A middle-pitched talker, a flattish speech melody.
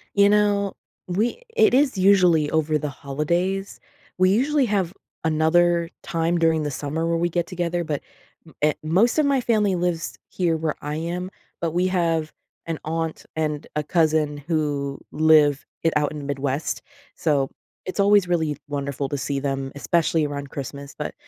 No: medium, 165 Hz; average, 3.5 semitones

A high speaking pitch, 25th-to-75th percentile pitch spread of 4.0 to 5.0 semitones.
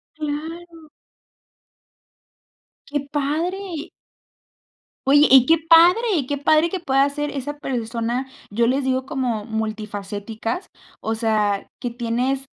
Yes: very high, 270 Hz; average, 4.7 semitones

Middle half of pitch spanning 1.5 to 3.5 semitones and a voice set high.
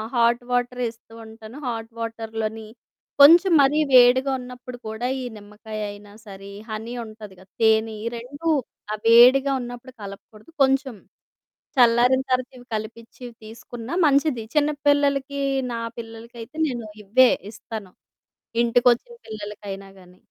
Yes: average, 2.8 semitones; high, 235 Hz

